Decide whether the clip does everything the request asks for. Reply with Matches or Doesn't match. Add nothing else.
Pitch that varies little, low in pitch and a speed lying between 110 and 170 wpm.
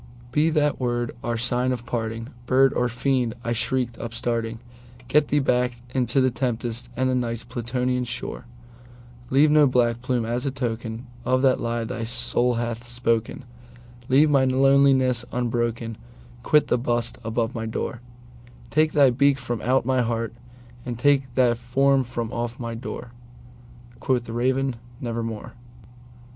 Matches